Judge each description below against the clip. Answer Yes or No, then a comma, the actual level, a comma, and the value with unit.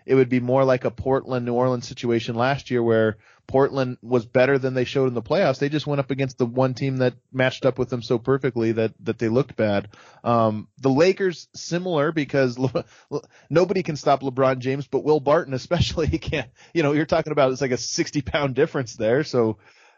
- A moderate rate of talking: No, fast, 215 wpm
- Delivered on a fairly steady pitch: Yes, narrow, 2.2 semitones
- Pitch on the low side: Yes, low, 130 Hz